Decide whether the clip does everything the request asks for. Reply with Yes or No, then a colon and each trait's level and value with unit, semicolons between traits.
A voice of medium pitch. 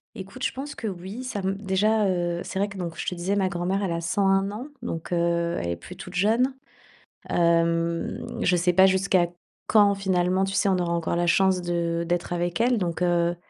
Yes: medium, 180 Hz